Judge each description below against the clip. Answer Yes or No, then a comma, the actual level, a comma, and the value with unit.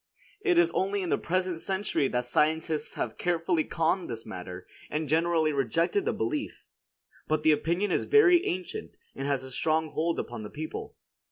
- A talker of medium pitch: Yes, medium, 160 Hz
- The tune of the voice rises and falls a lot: No, average, 4.2 semitones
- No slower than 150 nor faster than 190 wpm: Yes, average, 175 wpm